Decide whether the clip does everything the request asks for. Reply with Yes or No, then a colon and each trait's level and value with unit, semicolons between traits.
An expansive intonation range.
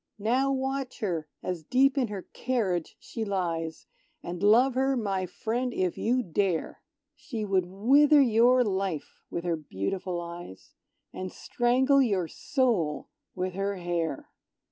Yes: wide, 6.3 semitones